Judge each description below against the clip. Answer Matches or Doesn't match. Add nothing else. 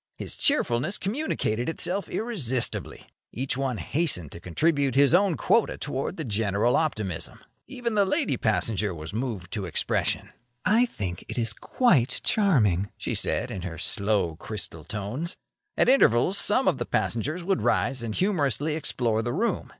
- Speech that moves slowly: Doesn't match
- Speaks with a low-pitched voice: Matches